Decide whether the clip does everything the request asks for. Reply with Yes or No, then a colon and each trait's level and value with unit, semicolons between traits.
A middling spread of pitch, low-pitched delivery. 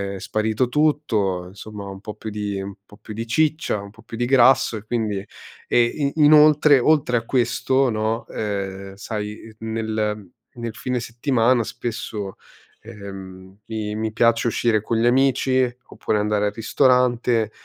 Yes: average, 3.0 semitones; low, 110 Hz